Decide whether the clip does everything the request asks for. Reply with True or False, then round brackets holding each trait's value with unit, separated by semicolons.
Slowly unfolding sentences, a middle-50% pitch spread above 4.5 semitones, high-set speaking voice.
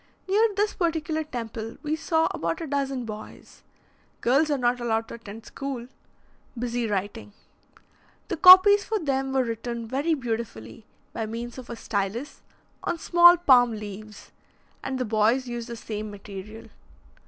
False (150 wpm; 5.3 semitones; 240 Hz)